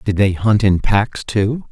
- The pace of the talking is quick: Yes, fast, 210 wpm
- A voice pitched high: No, low, 105 Hz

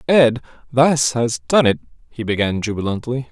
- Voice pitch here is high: No, low, 125 Hz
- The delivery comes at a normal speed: Yes, average, 145 wpm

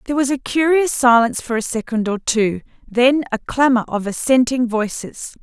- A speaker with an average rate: Yes, average, 175 wpm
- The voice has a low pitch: No, high, 245 Hz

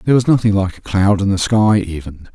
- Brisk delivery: Yes, fast, 255 wpm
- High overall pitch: No, low, 100 Hz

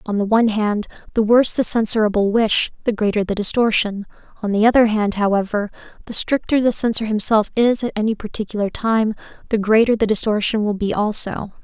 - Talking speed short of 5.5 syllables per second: No, 5.8 syllables/s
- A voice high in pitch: Yes, high, 215 Hz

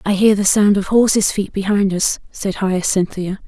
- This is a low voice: No, high, 200 Hz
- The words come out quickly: No, average, 190 wpm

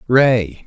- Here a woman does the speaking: No, male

